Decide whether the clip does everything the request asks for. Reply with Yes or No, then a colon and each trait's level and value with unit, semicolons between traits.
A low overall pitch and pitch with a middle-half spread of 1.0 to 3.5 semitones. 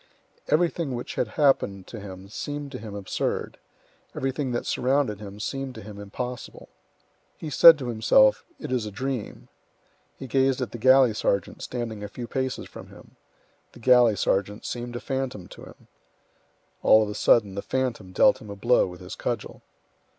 No: low, 120 Hz; average, 4.3 semitones